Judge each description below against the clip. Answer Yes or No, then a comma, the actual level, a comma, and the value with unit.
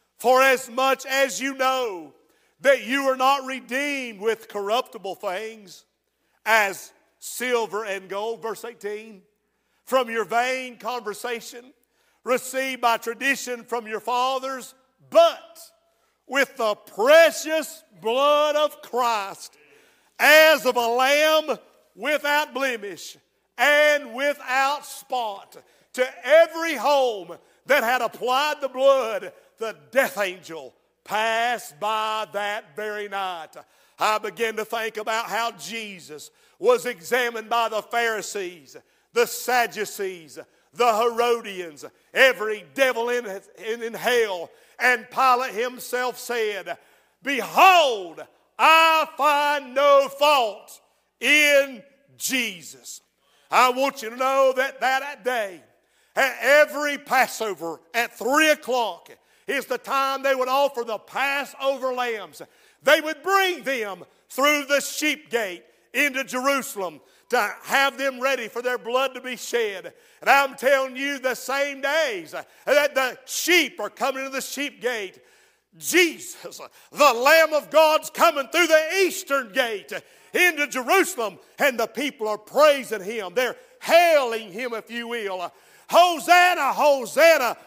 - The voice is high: Yes, very high, 260 Hz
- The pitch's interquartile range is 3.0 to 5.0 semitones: Yes, average, 4.1 semitones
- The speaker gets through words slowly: Yes, slow, 125 wpm